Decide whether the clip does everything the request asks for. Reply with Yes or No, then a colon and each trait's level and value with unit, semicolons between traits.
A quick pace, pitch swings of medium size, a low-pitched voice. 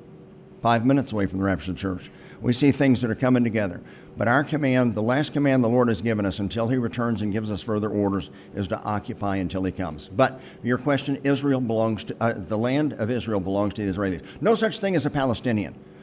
Yes: fast, 230 wpm; average, 4.5 semitones; low, 115 Hz